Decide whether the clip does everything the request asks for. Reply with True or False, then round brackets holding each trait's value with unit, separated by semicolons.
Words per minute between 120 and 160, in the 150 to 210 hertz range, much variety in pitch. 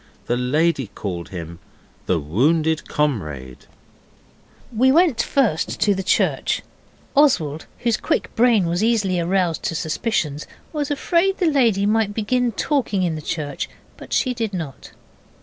True (140 wpm; 185 Hz; 8.1 semitones)